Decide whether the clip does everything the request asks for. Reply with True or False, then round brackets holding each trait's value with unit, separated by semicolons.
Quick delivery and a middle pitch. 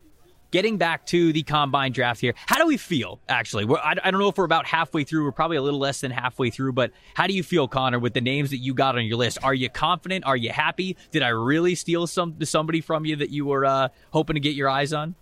True (270 wpm; 150 Hz)